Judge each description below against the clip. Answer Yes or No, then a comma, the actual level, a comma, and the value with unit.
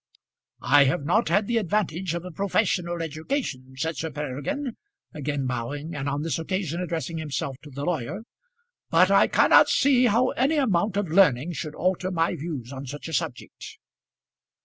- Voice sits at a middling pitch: Yes, medium, 165 Hz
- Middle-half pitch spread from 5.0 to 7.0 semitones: Yes, average, 5.3 semitones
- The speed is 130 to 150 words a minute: No, average, 170 wpm